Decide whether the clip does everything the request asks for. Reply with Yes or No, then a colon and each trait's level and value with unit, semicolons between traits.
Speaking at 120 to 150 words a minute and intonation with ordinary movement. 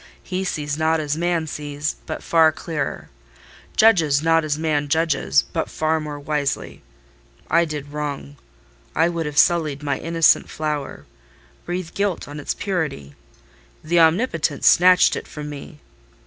No: average, 140 wpm; narrow, 2.3 semitones